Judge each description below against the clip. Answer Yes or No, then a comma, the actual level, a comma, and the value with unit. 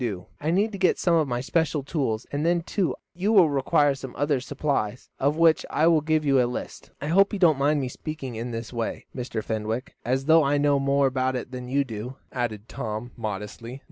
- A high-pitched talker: No, medium, 140 Hz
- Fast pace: Yes, fast, 220 wpm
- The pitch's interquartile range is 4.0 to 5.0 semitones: Yes, average, 4.3 semitones